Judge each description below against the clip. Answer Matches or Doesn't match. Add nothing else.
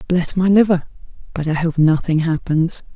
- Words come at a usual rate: Matches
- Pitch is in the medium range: Matches